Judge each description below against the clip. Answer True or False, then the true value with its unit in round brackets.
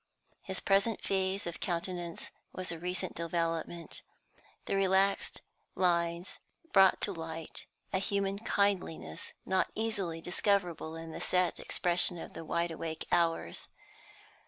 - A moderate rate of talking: False (120 wpm)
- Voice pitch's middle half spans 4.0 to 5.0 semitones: False (2.6 semitones)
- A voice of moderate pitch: True (175 Hz)